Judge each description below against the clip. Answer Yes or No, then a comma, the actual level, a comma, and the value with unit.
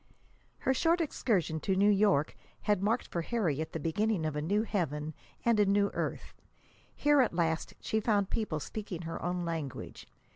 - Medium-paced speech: Yes, average, 175 wpm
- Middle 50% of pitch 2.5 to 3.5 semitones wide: No, average, 5.0 semitones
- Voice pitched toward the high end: Yes, high, 195 Hz